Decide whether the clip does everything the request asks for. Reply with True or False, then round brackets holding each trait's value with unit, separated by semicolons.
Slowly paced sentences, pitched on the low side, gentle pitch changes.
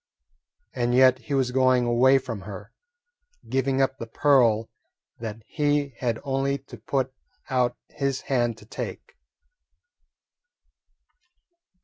True (115 wpm; 130 Hz; 2.3 semitones)